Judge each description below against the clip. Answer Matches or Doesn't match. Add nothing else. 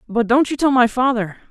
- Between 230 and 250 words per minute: Matches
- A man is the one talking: Doesn't match